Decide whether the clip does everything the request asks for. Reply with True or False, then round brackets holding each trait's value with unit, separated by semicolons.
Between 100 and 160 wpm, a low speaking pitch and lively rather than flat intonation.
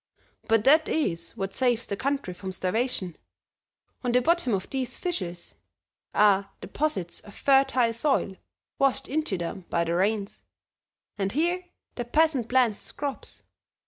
False (145 wpm; 235 Hz; 6.1 semitones)